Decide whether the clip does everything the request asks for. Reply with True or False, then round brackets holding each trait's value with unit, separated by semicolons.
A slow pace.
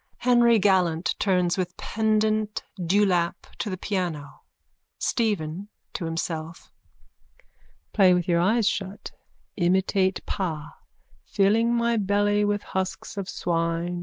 True (110 wpm)